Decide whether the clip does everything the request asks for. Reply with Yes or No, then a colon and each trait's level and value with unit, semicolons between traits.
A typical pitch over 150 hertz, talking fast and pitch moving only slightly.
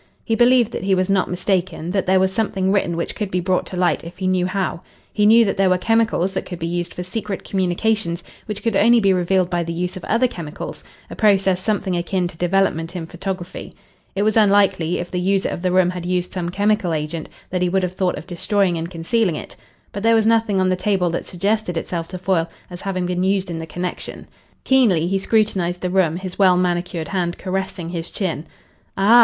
Yes: medium, 185 Hz; fast, 225 wpm; narrow, 2.1 semitones